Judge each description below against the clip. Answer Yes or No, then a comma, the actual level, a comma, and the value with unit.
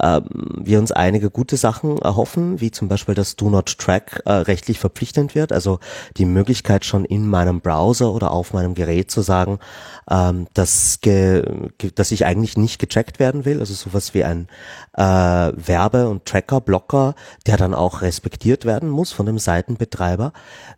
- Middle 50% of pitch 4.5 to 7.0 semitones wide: No, average, 4.1 semitones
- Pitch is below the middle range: Yes, low, 100 Hz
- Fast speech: No, average, 165 wpm